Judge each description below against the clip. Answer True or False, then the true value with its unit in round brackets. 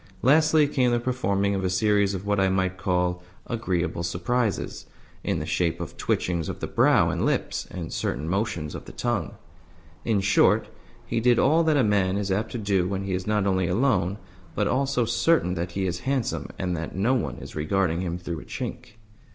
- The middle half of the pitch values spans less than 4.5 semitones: False (4.9 semitones)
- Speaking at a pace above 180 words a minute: True (200 wpm)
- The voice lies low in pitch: True (100 Hz)